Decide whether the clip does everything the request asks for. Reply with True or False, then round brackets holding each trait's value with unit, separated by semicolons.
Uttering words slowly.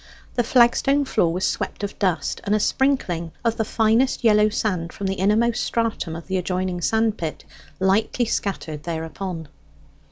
False (160 wpm)